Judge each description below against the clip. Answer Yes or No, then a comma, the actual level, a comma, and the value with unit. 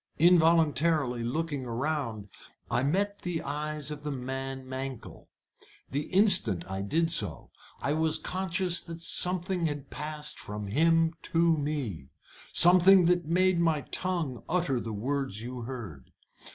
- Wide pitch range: No, average, 4.7 semitones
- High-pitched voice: No, medium, 150 Hz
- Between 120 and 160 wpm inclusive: Yes, slow, 135 wpm